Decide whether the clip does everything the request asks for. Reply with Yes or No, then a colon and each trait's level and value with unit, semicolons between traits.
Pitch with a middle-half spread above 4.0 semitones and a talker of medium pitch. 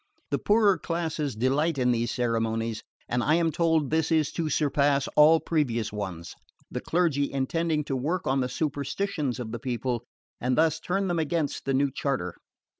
Yes: average, 4.6 semitones; medium, 145 Hz